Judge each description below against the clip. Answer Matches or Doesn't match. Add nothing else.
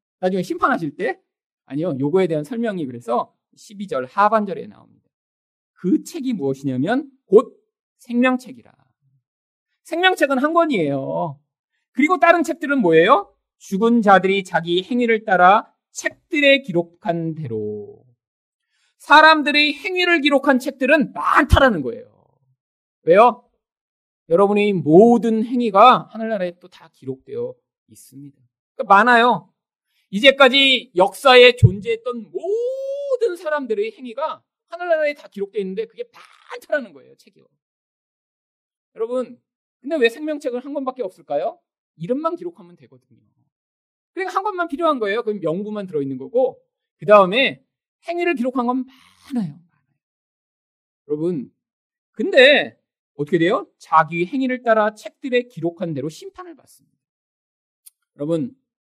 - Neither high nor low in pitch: Doesn't match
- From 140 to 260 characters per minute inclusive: Doesn't match